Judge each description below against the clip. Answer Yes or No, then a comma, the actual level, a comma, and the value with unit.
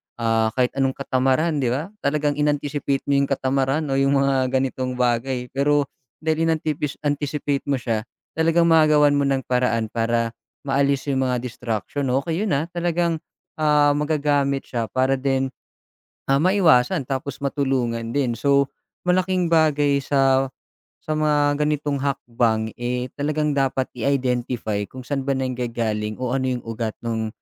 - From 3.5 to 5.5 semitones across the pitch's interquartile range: No, average, 2.9 semitones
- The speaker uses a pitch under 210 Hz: Yes, low, 135 Hz